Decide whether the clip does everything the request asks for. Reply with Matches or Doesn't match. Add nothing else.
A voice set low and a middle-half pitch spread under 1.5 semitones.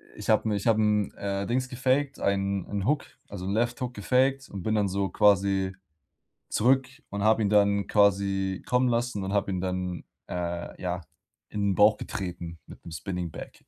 Doesn't match